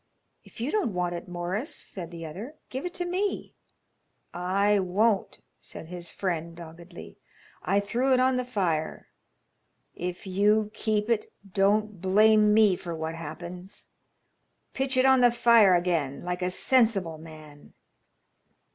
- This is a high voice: Yes, high, 195 Hz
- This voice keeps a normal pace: Yes, average, 145 wpm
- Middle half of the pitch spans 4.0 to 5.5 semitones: Yes, average, 4.6 semitones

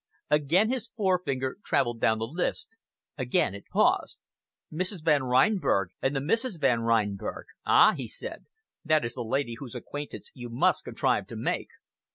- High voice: No, low, 135 Hz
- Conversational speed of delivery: Yes, average, 160 wpm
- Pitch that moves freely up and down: Yes, wide, 7.0 semitones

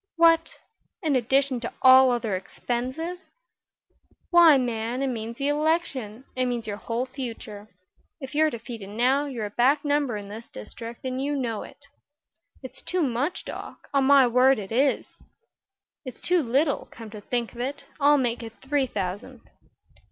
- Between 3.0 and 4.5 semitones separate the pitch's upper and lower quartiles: Yes, average, 3.5 semitones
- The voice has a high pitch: Yes, very high, 255 Hz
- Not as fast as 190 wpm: Yes, average, 165 wpm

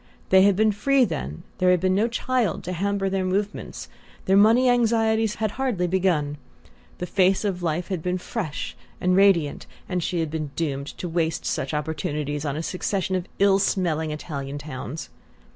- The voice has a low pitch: No, medium, 185 Hz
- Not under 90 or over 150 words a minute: No, average, 175 wpm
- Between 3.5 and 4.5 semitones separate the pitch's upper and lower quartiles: Yes, average, 4.2 semitones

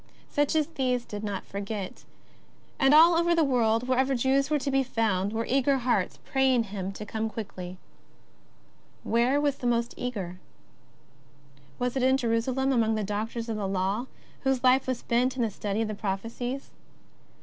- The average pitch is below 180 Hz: No, high, 240 Hz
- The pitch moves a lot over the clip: No, average, 3.9 semitones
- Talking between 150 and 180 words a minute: Yes, average, 170 wpm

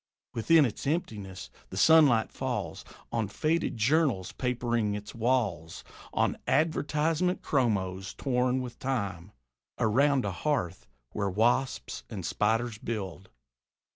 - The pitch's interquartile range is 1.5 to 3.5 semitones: No, wide, 5.4 semitones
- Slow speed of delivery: Yes, slow, 110 wpm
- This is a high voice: No, low, 120 Hz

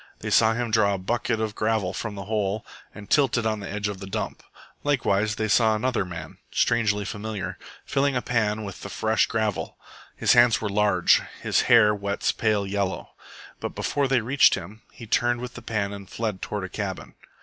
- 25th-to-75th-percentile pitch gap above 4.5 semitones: No, narrow, 2.4 semitones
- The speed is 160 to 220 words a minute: Yes, average, 200 wpm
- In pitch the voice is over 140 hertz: No, low, 110 Hz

